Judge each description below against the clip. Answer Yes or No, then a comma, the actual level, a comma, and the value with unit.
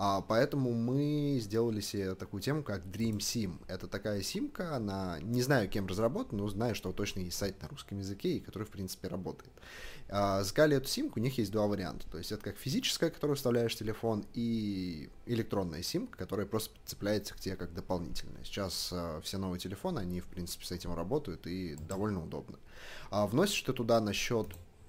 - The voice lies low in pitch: Yes, low, 100 Hz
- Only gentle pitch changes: No, average, 3.8 semitones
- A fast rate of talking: Yes, fast, 180 wpm